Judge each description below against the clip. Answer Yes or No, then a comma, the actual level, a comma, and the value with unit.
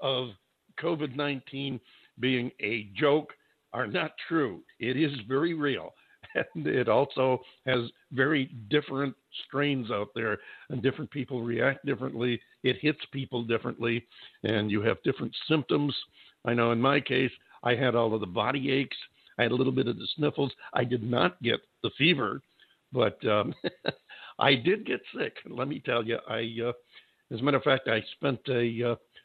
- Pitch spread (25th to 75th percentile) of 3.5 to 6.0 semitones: No, average, 2.8 semitones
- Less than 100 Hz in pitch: No, low, 130 Hz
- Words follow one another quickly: No, average, 170 wpm